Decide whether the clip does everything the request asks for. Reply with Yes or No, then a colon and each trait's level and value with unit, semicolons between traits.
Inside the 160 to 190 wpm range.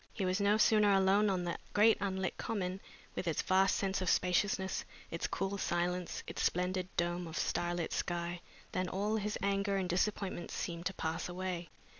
Yes: average, 175 wpm